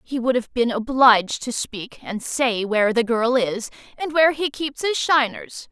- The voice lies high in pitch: Yes, high, 245 Hz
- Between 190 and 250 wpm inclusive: Yes, average, 200 wpm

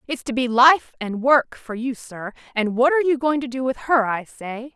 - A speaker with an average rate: No, fast, 250 wpm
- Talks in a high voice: Yes, very high, 250 Hz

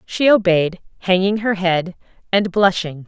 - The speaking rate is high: No, slow, 135 wpm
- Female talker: Yes, female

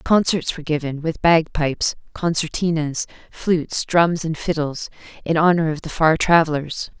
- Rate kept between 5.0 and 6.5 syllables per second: No, 4.8 syllables/s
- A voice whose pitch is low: No, medium, 160 Hz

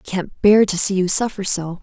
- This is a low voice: No, high, 190 Hz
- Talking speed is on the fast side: Yes, fast, 265 wpm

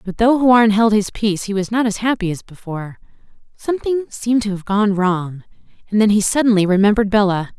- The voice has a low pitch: No, high, 210 Hz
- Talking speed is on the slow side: No, average, 200 wpm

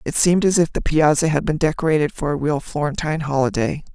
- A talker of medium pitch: Yes, medium, 155 Hz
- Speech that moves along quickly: Yes, fast, 215 wpm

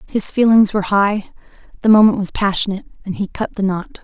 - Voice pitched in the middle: No, high, 200 Hz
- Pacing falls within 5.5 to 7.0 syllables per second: Yes, 6.0 syllables/s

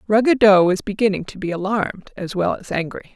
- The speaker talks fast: No, average, 190 wpm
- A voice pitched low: No, high, 195 Hz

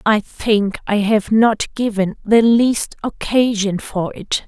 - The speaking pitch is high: Yes, high, 215 Hz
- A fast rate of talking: No, average, 145 wpm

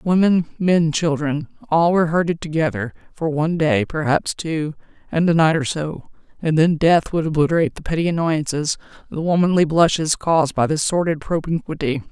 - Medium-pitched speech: Yes, medium, 160 Hz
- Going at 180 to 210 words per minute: No, average, 160 wpm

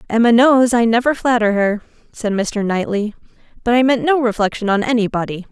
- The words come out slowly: No, average, 185 wpm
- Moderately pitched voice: No, high, 225 Hz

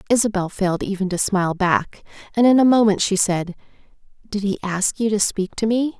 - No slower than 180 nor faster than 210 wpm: Yes, average, 200 wpm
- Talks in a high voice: Yes, high, 200 Hz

